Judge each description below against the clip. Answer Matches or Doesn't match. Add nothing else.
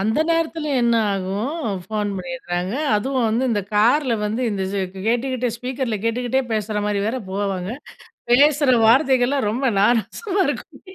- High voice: Matches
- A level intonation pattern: Doesn't match